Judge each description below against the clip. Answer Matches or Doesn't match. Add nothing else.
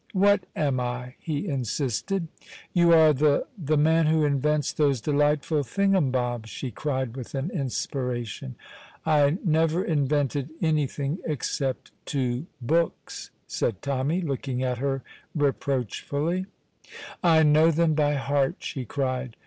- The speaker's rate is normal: Doesn't match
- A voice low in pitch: Doesn't match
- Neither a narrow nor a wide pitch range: Matches